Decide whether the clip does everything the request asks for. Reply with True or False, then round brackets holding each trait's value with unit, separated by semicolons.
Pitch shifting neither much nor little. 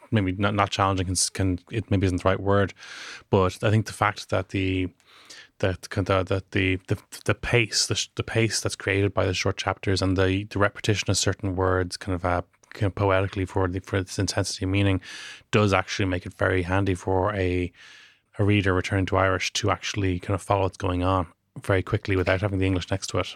False (1.3 semitones)